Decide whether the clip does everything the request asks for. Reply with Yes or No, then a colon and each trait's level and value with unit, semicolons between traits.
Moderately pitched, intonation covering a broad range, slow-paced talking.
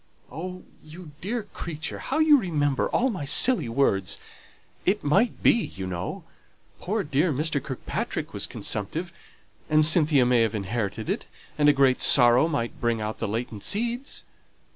No: medium, 145 Hz; wide, 7.6 semitones; average, 155 wpm